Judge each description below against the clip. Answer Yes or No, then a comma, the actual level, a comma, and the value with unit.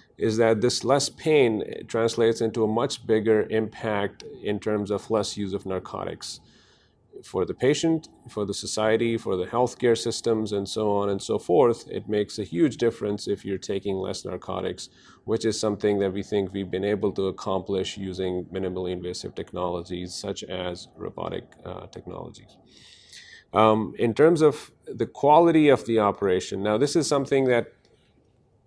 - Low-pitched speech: Yes, low, 105 Hz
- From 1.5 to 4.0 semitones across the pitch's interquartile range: Yes, average, 2.9 semitones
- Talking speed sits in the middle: Yes, average, 165 wpm